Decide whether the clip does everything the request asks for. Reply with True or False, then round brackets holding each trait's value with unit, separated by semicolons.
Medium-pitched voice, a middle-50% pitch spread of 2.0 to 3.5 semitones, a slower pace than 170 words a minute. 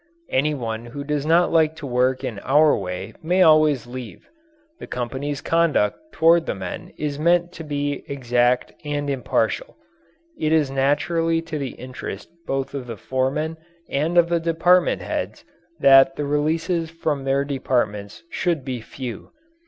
False (145 Hz; 4.0 semitones; 155 wpm)